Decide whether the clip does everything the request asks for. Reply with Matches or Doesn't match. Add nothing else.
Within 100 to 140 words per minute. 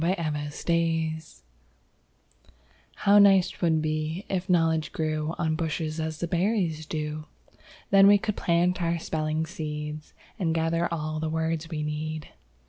Matches